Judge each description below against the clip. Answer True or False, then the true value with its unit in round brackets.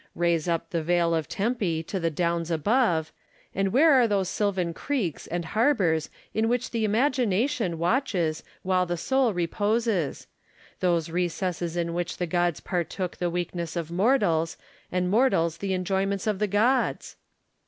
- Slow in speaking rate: False (155 wpm)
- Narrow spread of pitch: False (4.3 semitones)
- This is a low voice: False (180 Hz)